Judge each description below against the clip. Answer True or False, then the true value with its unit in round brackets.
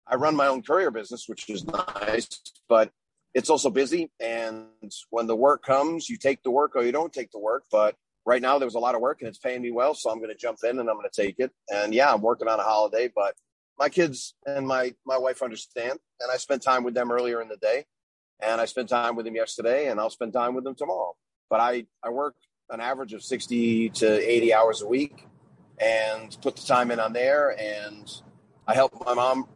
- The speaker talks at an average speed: False (235 wpm)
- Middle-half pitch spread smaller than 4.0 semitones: True (3.1 semitones)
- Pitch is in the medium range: False (125 Hz)